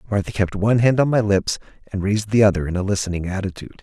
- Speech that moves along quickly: Yes, fast, 235 wpm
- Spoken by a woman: No, male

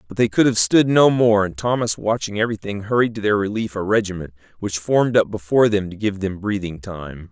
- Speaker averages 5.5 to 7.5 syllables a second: Yes, 5.8 syllables/s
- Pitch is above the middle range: No, low, 105 Hz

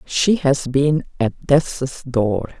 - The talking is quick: No, average, 140 wpm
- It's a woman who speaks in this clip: Yes, female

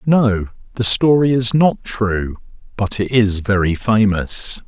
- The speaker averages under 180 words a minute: Yes, average, 140 wpm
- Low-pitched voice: Yes, low, 110 Hz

